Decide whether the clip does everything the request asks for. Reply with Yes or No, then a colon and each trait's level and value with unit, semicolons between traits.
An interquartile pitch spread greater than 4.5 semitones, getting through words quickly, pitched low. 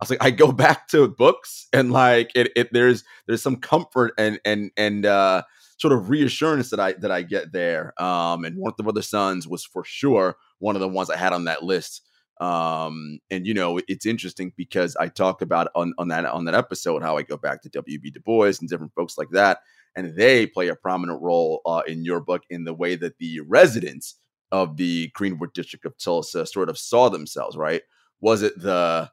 Yes: average, 4.9 semitones; fast, 220 wpm; very low, 95 Hz